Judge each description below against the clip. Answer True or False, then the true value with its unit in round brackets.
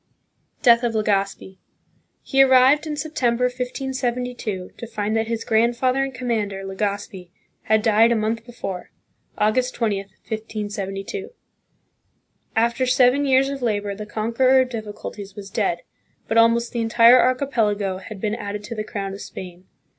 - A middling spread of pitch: True (3.4 semitones)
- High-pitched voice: True (225 Hz)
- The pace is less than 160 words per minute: True (145 wpm)